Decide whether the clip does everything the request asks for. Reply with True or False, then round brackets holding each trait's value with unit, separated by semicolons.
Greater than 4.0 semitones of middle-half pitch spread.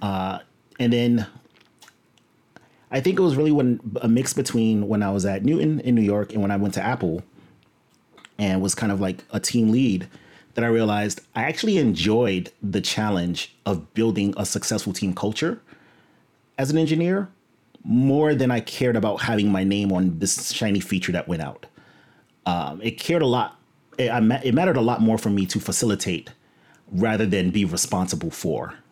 False (3.5 semitones)